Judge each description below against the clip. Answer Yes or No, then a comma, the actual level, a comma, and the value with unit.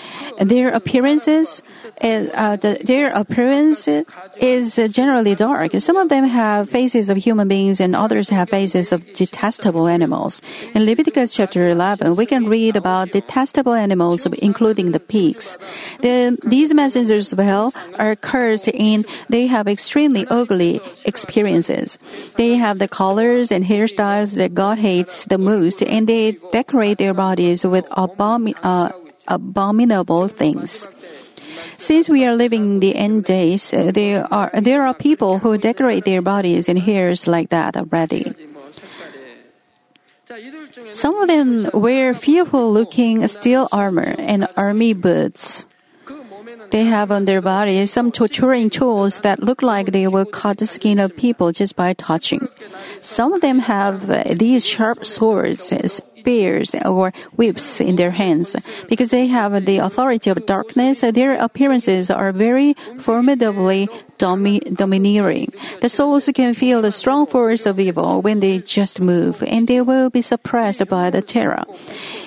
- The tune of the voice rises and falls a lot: No, average, 4.1 semitones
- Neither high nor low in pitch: No, high, 215 Hz